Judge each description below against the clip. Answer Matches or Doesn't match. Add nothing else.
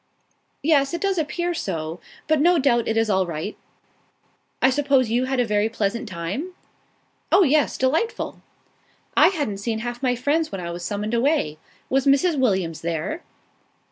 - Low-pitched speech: Doesn't match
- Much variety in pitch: Matches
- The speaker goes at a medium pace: Matches